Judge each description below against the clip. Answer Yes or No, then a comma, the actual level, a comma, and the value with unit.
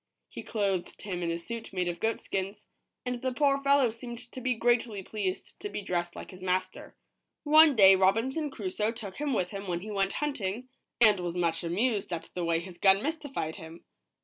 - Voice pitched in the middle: No, high, 200 Hz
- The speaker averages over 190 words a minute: Yes, average, 200 wpm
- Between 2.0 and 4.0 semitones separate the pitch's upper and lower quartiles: No, average, 5.2 semitones